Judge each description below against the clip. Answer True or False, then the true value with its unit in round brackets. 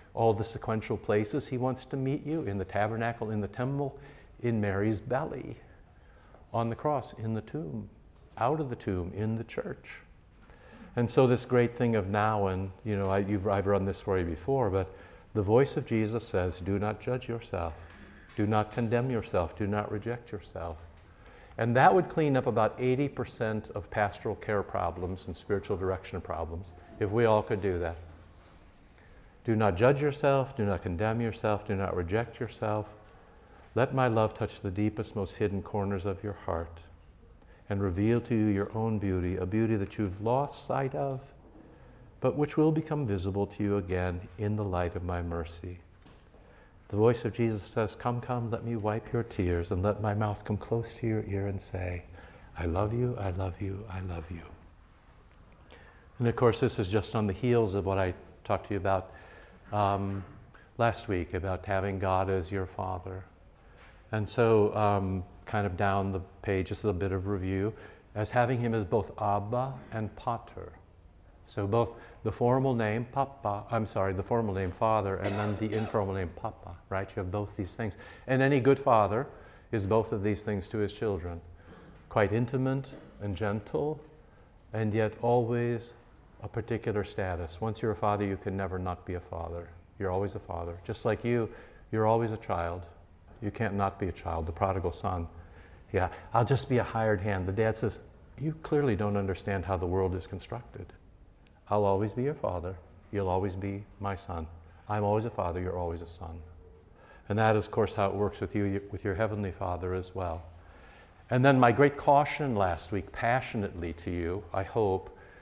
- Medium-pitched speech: False (105 Hz)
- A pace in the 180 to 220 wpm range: True (185 wpm)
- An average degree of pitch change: True (3.6 semitones)